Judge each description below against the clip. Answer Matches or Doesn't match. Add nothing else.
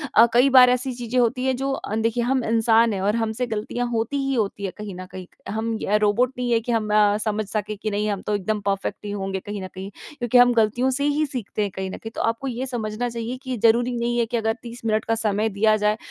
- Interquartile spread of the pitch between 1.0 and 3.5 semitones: Matches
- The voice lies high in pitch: Matches